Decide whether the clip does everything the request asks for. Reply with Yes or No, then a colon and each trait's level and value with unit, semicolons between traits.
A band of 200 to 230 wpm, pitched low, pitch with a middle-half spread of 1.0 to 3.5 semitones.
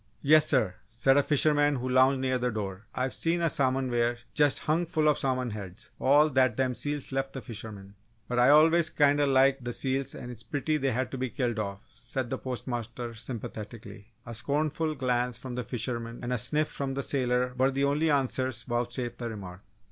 Yes: fast, 205 wpm; low, 130 Hz; average, 2.9 semitones